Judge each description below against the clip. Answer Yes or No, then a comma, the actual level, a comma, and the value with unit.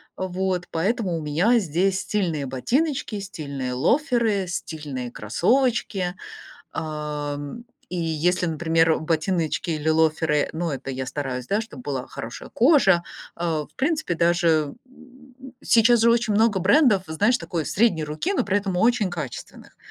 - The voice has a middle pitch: Yes, medium, 175 Hz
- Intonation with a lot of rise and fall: Yes, wide, 6.2 semitones